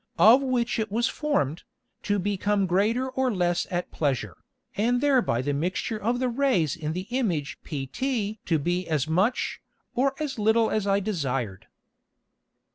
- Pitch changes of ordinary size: No, wide, 7.0 semitones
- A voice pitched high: Yes, high, 205 Hz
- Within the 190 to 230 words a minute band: No, average, 155 wpm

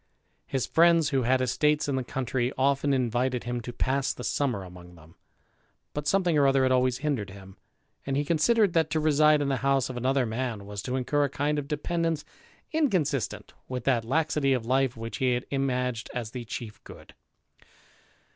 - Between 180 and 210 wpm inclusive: Yes, average, 190 wpm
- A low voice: Yes, low, 130 Hz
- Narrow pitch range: No, average, 3.2 semitones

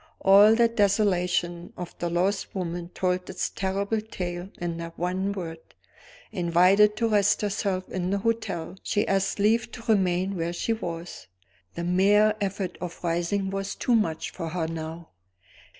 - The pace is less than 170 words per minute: Yes, average, 155 wpm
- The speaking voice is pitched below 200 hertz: Yes, high, 190 Hz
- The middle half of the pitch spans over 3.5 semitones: No, average, 2.8 semitones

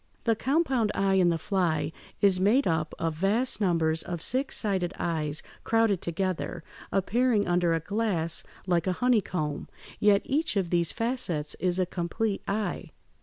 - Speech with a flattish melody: No, average, 4.7 semitones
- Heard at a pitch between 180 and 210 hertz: Yes, medium, 185 Hz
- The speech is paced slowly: No, average, 155 wpm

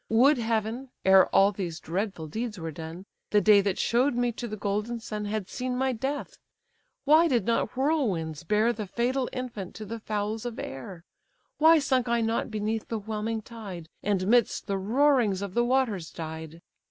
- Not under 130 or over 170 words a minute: No, average, 180 wpm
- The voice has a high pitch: Yes, high, 220 Hz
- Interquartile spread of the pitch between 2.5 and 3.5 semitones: No, average, 3.9 semitones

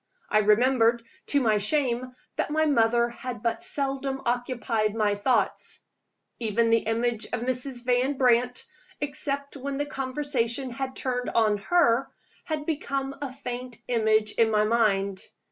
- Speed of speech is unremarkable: Yes, average, 145 wpm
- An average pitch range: Yes, average, 3.1 semitones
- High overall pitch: Yes, high, 245 Hz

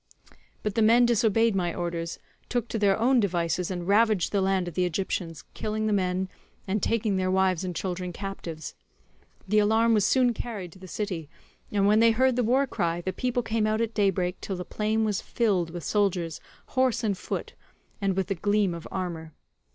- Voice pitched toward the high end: Yes, high, 195 Hz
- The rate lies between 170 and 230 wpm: Yes, average, 200 wpm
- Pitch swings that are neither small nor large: Yes, average, 3.5 semitones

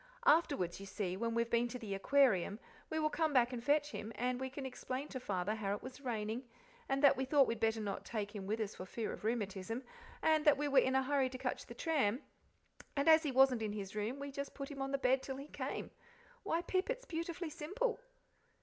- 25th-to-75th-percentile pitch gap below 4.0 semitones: No, average, 4.8 semitones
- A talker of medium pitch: No, very high, 260 Hz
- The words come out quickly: Yes, fast, 240 wpm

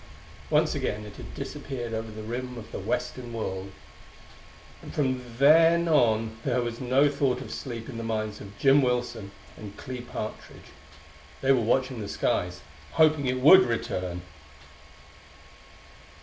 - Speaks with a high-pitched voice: No, low, 120 Hz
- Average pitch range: Yes, average, 3.4 semitones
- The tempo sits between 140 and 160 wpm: Yes, average, 150 wpm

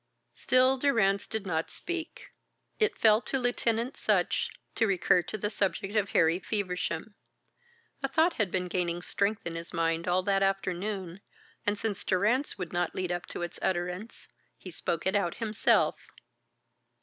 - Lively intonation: No, average, 3.8 semitones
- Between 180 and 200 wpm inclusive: No, average, 160 wpm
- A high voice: Yes, high, 195 Hz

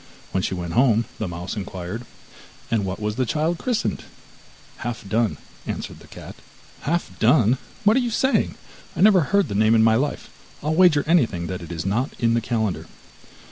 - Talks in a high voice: No, low, 115 Hz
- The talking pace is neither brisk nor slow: Yes, average, 180 wpm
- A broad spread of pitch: Yes, wide, 7.5 semitones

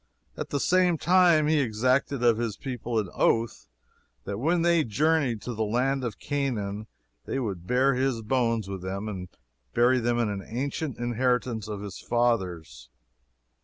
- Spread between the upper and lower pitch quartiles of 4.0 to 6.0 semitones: Yes, average, 4.3 semitones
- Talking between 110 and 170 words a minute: Yes, average, 165 wpm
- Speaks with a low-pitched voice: Yes, low, 120 Hz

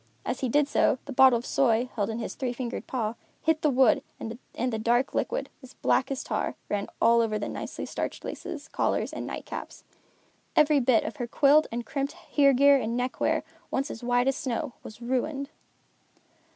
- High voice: Yes, very high, 255 Hz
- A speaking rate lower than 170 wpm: No, average, 190 wpm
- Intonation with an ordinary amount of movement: Yes, average, 3.0 semitones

